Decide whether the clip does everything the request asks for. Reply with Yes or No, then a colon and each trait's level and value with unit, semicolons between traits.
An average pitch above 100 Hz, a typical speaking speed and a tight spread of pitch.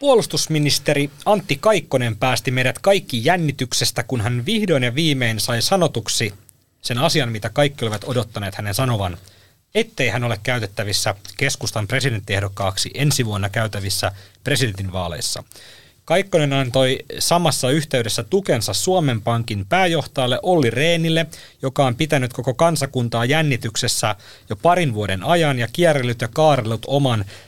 No: low, 130 Hz; average, 125 wpm; average, 5.1 semitones